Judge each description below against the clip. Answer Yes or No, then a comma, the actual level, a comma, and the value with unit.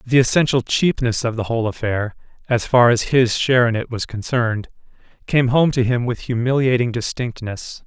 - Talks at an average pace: Yes, average, 160 wpm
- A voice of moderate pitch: No, low, 120 Hz